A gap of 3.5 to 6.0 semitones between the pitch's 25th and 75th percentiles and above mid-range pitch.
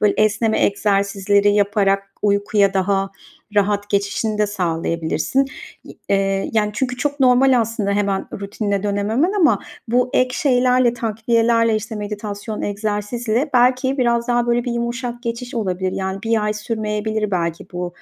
No: average, 3.0 semitones; high, 215 Hz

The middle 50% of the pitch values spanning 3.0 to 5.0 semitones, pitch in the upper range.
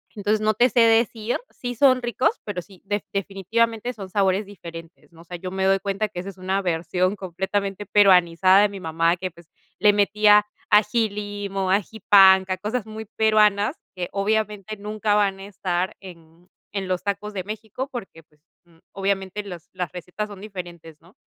No: narrow, 2.4 semitones; high, 195 Hz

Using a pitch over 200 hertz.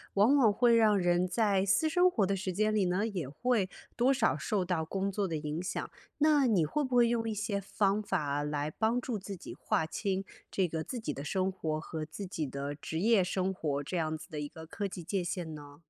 No: high, 190 Hz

